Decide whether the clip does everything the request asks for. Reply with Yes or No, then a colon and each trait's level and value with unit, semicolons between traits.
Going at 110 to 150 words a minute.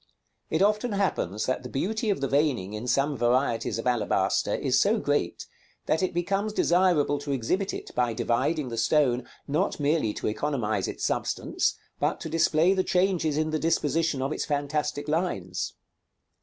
No: average, 170 wpm